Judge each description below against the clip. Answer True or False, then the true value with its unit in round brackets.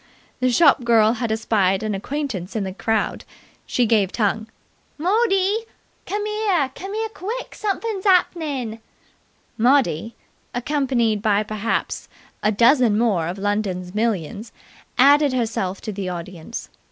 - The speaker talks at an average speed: False (120 wpm)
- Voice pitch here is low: False (230 Hz)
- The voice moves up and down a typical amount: False (6.4 semitones)